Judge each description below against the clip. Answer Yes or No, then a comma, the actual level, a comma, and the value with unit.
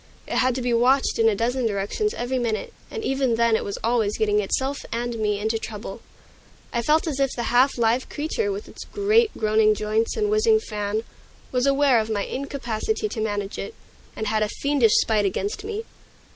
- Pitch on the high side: Yes, high, 235 Hz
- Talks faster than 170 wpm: Yes, average, 200 wpm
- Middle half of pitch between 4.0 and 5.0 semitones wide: Yes, average, 4.4 semitones